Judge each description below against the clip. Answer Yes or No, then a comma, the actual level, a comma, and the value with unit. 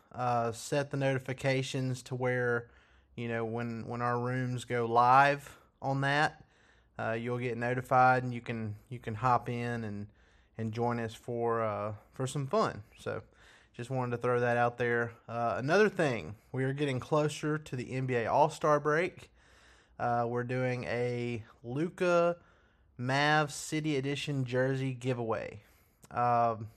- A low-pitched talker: Yes, low, 125 Hz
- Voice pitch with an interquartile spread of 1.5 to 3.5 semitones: Yes, narrow, 2.4 semitones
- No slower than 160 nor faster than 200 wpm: No, average, 150 wpm